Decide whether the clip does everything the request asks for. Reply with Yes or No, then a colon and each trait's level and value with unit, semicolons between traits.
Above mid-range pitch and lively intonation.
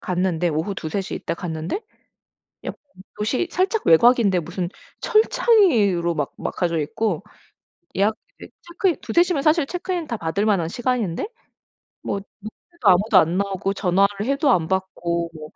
Yes: high, 195 Hz; wide, 6.7 semitones